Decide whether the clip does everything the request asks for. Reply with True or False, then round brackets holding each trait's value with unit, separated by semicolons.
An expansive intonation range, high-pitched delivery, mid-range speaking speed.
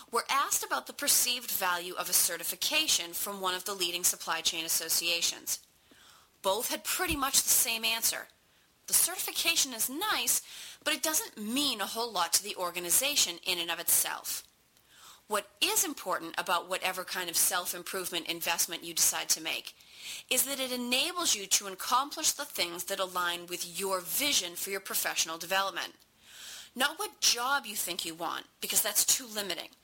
True (7.3 semitones; 195 Hz; 170 wpm)